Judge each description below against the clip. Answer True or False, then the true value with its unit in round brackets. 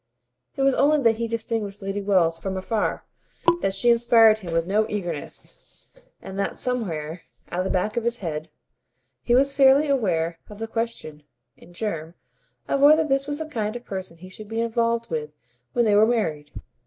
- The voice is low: False (215 Hz)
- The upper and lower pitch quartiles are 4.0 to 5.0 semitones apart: True (4.7 semitones)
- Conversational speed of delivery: True (190 wpm)